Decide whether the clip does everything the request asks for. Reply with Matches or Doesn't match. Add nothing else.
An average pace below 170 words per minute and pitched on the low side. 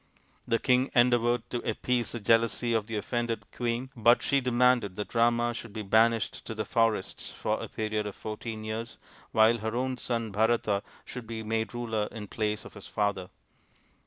Doesn't match